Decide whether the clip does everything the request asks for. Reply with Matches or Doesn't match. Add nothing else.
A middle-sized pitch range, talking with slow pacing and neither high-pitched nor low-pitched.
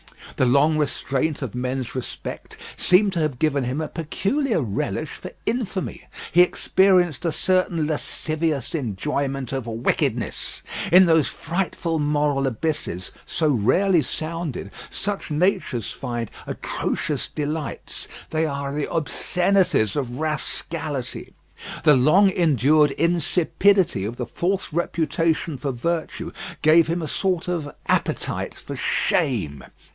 Matches